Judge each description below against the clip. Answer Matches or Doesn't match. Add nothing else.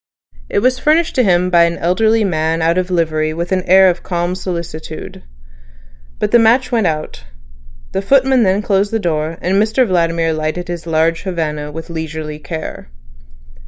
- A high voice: Doesn't match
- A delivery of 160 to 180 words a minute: Matches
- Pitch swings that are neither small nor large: Matches